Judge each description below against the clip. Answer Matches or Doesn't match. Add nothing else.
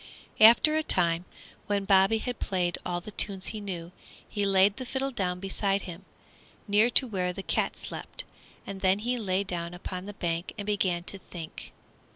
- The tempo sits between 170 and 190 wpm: Matches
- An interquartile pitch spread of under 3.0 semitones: Matches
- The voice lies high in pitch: Matches